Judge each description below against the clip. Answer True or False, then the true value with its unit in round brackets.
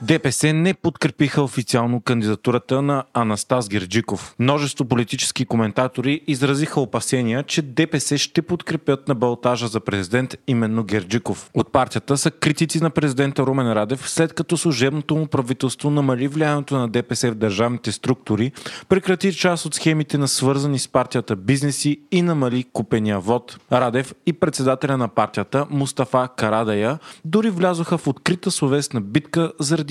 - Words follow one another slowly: False (140 wpm)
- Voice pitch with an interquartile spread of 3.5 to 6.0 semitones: True (4.0 semitones)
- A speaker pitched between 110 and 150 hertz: True (135 Hz)